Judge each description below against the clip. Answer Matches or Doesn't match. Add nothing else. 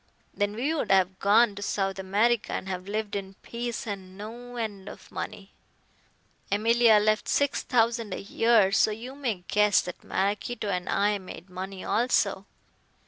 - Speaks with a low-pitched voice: Doesn't match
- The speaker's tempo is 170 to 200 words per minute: Doesn't match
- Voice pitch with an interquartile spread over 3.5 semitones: Doesn't match